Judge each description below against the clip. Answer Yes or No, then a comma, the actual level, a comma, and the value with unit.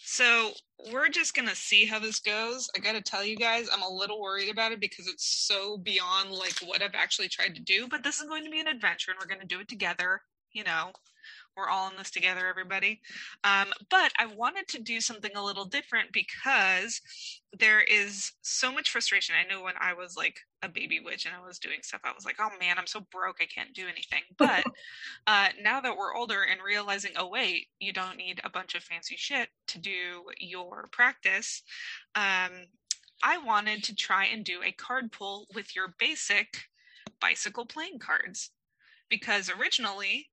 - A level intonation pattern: No, average, 3.9 semitones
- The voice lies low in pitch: No, high, 205 Hz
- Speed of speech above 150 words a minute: Yes, fast, 205 wpm